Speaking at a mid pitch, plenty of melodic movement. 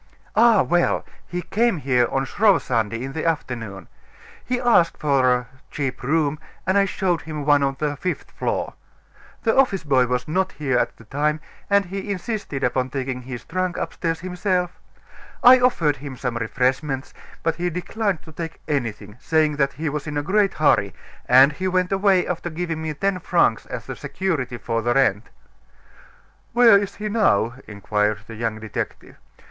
Yes: medium, 150 Hz; wide, 6.4 semitones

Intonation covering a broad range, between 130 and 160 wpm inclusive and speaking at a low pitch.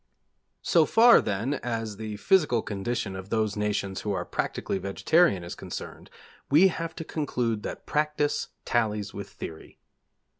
Yes: wide, 6.5 semitones; average, 145 wpm; low, 110 Hz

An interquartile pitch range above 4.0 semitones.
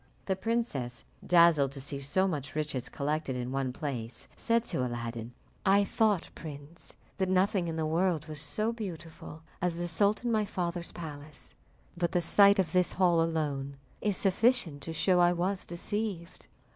Yes: average, 4.9 semitones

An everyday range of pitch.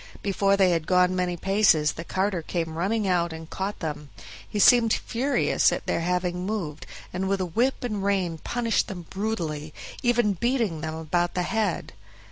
Yes: average, 3.9 semitones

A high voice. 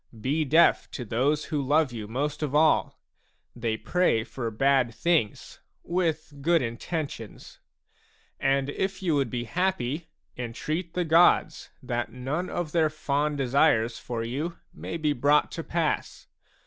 No: medium, 145 Hz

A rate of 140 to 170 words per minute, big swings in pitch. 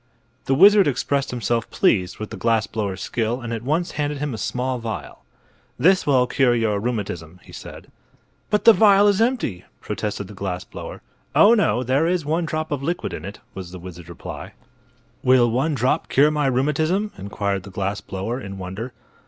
No: average, 185 wpm; wide, 7.0 semitones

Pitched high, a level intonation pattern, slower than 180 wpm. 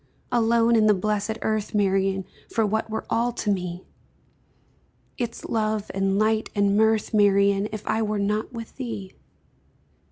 Yes: high, 215 Hz; narrow, 1.8 semitones; average, 150 wpm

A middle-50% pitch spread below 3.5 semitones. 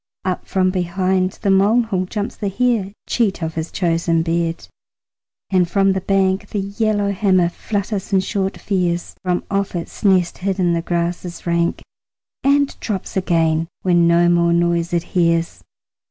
Yes: narrow, 2.5 semitones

